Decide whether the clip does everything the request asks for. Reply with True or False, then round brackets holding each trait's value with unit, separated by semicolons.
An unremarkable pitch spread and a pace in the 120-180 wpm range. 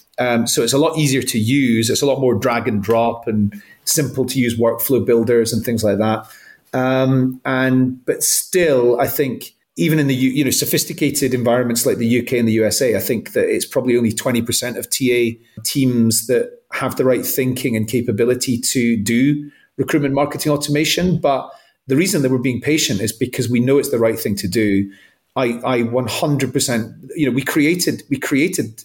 False (3.0 semitones; 200 wpm)